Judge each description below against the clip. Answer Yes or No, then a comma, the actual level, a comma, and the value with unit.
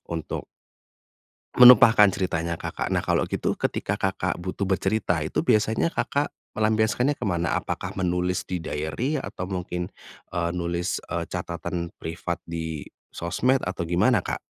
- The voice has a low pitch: Yes, very low, 90 Hz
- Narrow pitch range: No, average, 4.1 semitones